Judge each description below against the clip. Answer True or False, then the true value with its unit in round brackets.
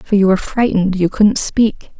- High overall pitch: True (200 Hz)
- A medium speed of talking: False (210 wpm)